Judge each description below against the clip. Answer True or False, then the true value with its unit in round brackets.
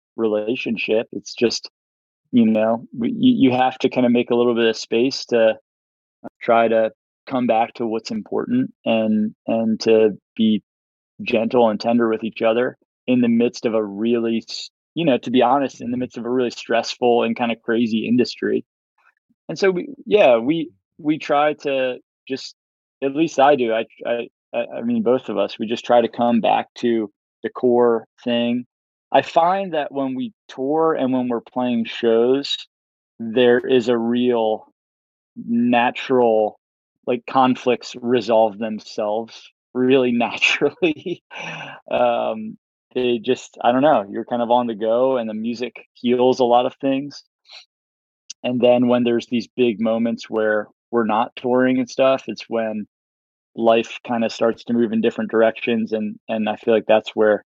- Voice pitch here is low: True (120 Hz)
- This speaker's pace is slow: False (170 wpm)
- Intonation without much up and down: True (2.3 semitones)